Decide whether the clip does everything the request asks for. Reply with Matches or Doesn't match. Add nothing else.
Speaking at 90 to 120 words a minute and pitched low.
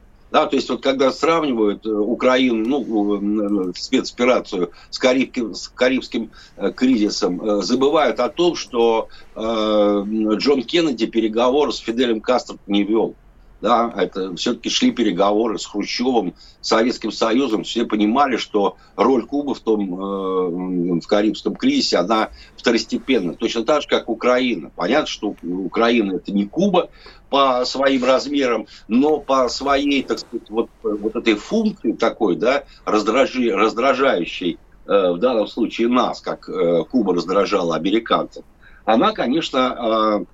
Doesn't match